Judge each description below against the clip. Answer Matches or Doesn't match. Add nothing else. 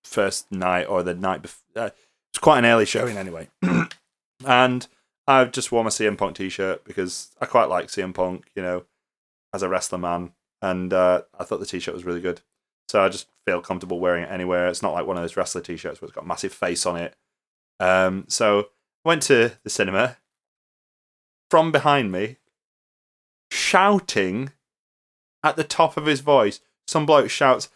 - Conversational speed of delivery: Matches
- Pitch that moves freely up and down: Matches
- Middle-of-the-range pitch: Doesn't match